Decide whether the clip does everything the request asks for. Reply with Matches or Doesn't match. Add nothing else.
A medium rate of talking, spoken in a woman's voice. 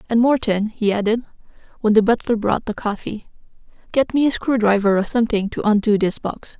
Matches